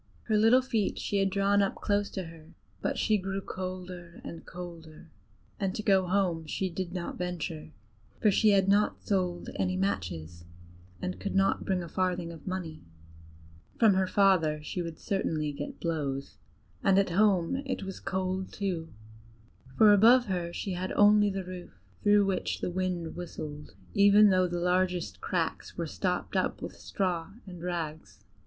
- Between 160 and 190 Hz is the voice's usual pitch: Yes, medium, 185 Hz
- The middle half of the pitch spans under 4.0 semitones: Yes, average, 2.8 semitones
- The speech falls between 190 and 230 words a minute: No, average, 165 wpm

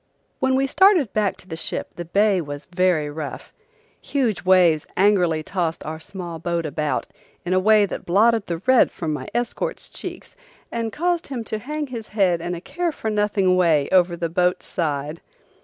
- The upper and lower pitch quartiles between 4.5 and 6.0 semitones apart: Yes, average, 5.1 semitones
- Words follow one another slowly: No, average, 185 wpm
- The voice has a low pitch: No, medium, 185 Hz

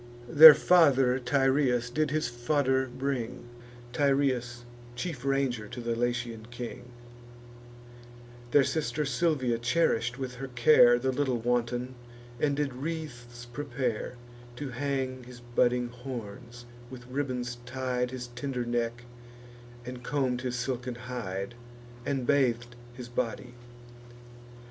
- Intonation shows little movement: Yes, narrow, 2.1 semitones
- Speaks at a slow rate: Yes, slow, 115 wpm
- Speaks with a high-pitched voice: No, low, 125 Hz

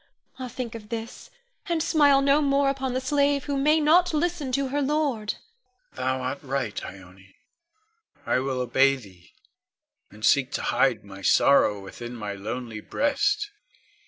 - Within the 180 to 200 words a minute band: No, average, 160 wpm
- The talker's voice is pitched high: Yes, high, 230 Hz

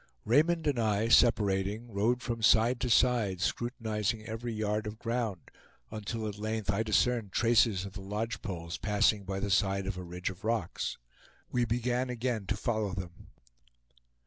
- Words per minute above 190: No, average, 165 wpm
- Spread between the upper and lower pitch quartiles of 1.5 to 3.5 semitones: Yes, average, 3.0 semitones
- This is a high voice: No, low, 110 Hz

